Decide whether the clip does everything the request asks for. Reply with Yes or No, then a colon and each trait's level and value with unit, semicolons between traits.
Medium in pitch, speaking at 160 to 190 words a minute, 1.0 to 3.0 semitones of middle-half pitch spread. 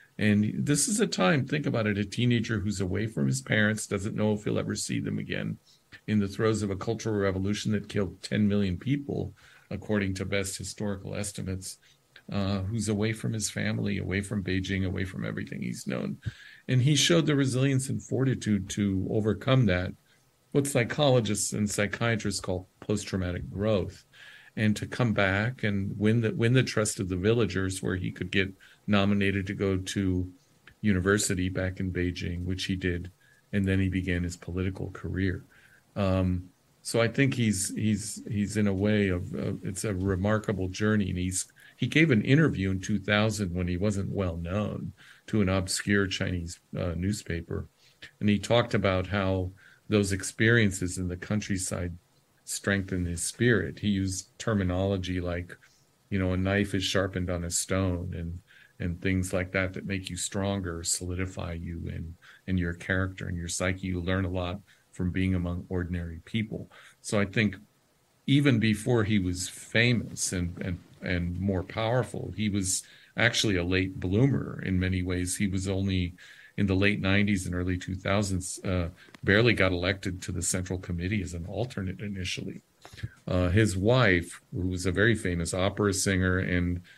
No: low, 100 Hz; average, 170 wpm; narrow, 2.6 semitones